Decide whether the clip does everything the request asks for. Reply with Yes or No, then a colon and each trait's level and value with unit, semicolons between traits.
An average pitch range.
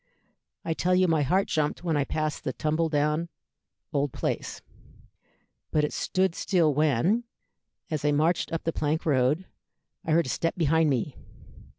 No: narrow, 2.3 semitones